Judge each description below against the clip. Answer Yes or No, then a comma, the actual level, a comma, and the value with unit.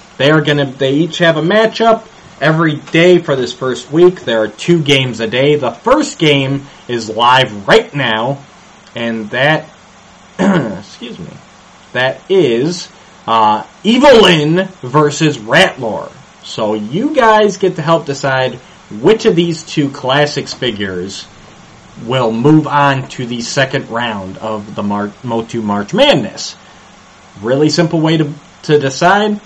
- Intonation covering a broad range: Yes, wide, 6.1 semitones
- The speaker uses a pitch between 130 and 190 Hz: Yes, medium, 140 Hz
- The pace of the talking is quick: No, average, 140 wpm